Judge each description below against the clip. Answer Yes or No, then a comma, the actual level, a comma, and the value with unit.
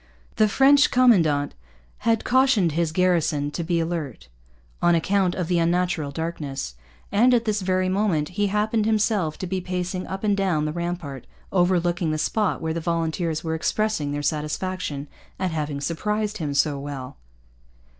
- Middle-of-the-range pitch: Yes, medium, 175 Hz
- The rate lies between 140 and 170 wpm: Yes, average, 160 wpm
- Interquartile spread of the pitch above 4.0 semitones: Yes, average, 4.5 semitones